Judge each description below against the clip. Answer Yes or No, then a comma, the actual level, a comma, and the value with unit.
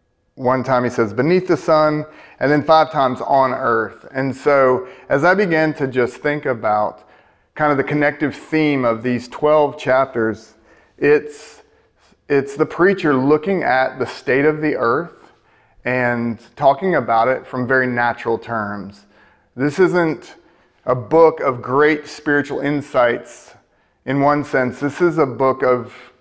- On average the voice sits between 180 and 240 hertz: No, low, 135 Hz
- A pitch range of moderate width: Yes, average, 3.7 semitones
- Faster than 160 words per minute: No, average, 150 wpm